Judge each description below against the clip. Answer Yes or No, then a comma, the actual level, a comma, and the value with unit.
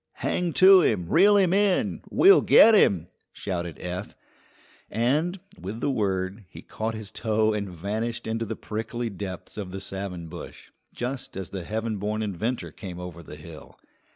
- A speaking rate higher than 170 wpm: No, average, 165 wpm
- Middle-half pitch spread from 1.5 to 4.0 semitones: No, average, 4.5 semitones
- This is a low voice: Yes, low, 105 Hz